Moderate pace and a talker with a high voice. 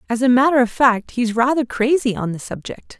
No: fast, 220 wpm; high, 245 Hz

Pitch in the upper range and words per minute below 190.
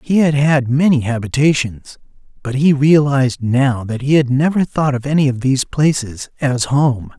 No: low, 135 Hz; average, 175 wpm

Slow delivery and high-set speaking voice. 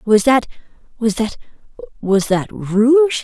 Yes: slow, 95 wpm; high, 230 Hz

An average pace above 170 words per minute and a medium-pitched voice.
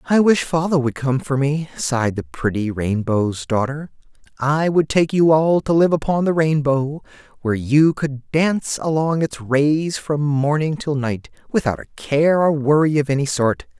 Yes: average, 180 wpm; medium, 145 Hz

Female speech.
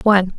Yes: female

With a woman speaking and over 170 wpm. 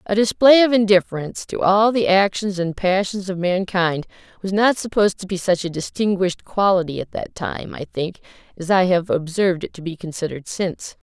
Yes: female; average, 190 wpm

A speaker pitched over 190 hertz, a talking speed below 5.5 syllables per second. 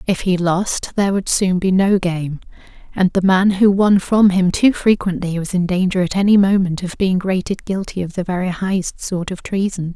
No: medium, 185 Hz; 5.0 syllables/s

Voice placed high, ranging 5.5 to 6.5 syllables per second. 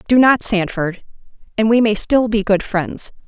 No: high, 215 Hz; 4.4 syllables/s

